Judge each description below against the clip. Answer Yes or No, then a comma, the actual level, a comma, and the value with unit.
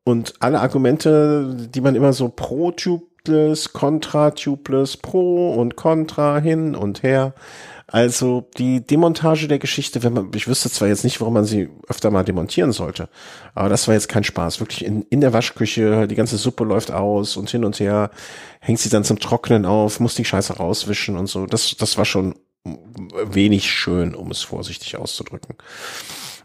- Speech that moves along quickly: No, average, 170 wpm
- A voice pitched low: Yes, low, 120 Hz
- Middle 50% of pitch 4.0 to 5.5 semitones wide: Yes, average, 5.2 semitones